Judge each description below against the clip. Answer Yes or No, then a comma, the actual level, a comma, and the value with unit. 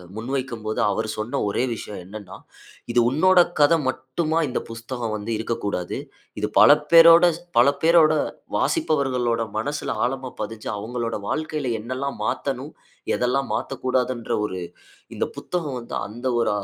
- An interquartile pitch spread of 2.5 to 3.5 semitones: No, average, 3.9 semitones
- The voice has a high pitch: No, low, 125 Hz